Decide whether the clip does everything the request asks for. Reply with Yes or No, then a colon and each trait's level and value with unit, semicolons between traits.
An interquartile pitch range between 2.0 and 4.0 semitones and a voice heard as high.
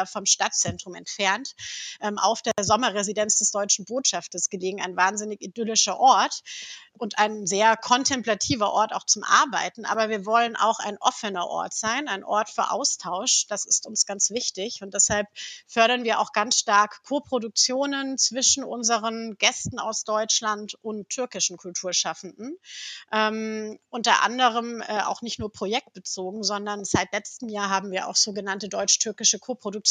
Yes: narrow, 2.5 semitones; high, 215 Hz